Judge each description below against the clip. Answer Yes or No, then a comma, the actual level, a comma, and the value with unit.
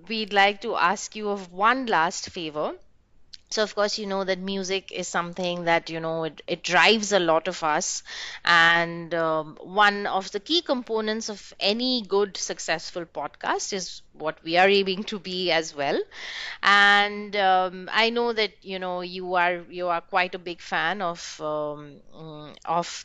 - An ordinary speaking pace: Yes, average, 175 wpm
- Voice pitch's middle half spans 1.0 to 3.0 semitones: No, average, 3.6 semitones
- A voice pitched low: No, medium, 185 Hz